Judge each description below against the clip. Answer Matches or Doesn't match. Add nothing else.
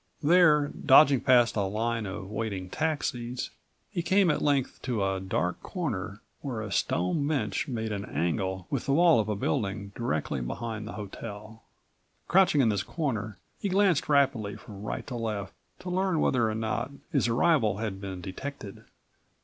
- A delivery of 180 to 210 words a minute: Doesn't match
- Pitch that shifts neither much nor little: Doesn't match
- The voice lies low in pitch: Matches